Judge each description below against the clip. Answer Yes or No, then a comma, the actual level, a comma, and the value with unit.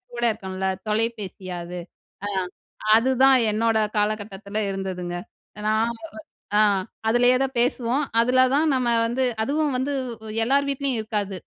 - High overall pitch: Yes, high, 230 Hz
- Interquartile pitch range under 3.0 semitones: No, average, 4.1 semitones